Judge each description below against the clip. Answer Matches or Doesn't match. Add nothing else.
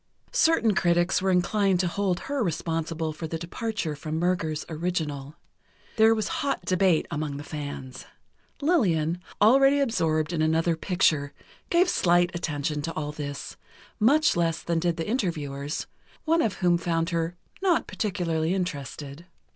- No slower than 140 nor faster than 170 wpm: Matches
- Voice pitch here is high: Doesn't match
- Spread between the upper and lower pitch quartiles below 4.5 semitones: Matches